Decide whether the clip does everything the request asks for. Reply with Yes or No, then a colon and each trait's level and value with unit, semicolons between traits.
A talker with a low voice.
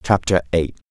Yes: very low, 80 Hz